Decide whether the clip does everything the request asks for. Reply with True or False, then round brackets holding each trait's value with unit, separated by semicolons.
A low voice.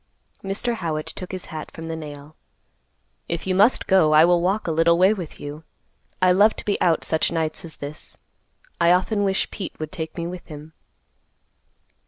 False (170 Hz)